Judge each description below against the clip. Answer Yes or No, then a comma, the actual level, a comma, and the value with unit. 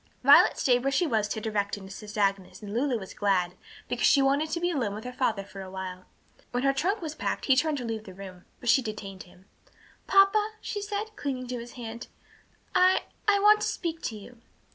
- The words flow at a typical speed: No, fast, 225 wpm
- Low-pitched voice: No, high, 245 Hz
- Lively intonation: Yes, wide, 7.5 semitones